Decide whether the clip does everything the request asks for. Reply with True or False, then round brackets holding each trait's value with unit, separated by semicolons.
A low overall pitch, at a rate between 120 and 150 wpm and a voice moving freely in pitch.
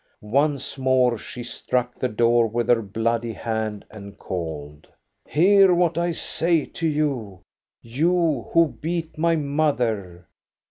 True (125 Hz; 140 wpm; 6.1 semitones)